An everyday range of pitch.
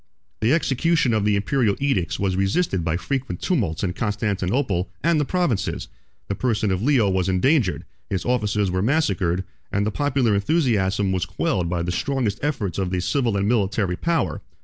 No: wide, 6.1 semitones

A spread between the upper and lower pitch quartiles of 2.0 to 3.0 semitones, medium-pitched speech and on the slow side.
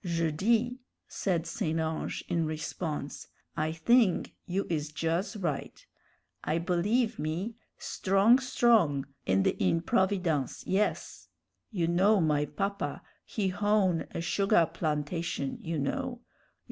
No: average, 4.6 semitones; medium, 175 Hz; slow, 120 wpm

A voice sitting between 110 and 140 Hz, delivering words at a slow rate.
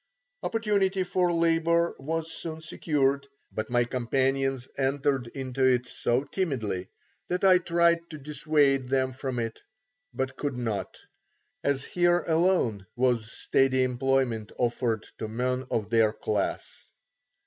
Yes: low, 135 Hz; slow, 125 wpm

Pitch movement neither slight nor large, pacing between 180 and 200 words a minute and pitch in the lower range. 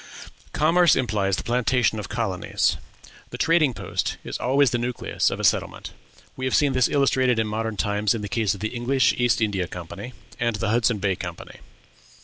Yes: average, 3.7 semitones; average, 185 wpm; low, 115 Hz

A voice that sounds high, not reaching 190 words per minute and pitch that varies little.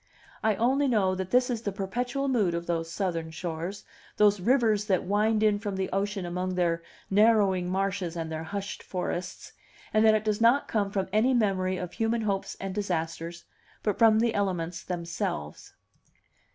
No: high, 195 Hz; average, 175 wpm; average, 3.4 semitones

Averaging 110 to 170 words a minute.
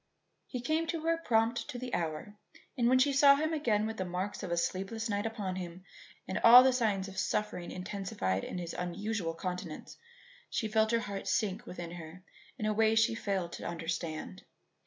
No: average, 185 wpm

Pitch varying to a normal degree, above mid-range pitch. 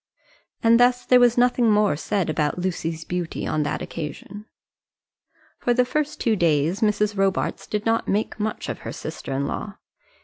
No: wide, 5.7 semitones; high, 210 Hz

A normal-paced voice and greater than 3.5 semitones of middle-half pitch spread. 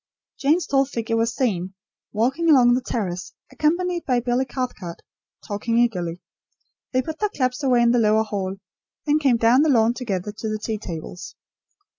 Yes: average, 170 wpm; average, 4.0 semitones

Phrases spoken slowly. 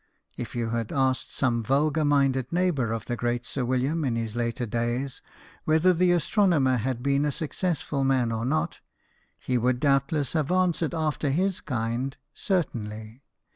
No: average, 160 wpm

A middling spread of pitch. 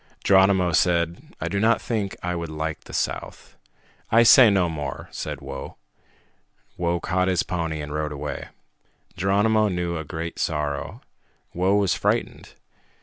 Yes: average, 3.4 semitones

